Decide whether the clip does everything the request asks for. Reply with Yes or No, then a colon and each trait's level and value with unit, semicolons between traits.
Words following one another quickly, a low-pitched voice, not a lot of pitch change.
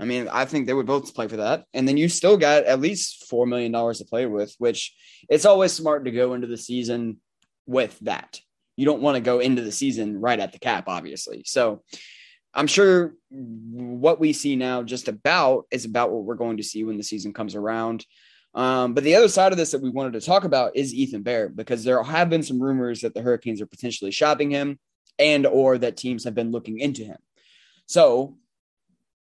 No: fast, 220 wpm; low, 125 Hz; average, 4.0 semitones